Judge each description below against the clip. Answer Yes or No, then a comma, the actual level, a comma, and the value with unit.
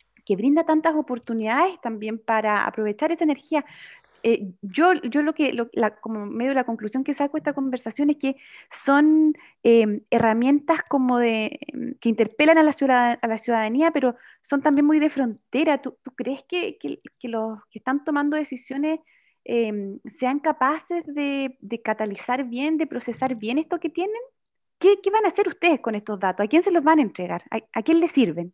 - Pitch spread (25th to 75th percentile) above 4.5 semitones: Yes, average, 5.1 semitones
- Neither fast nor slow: No, fast, 195 wpm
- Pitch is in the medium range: No, very high, 265 Hz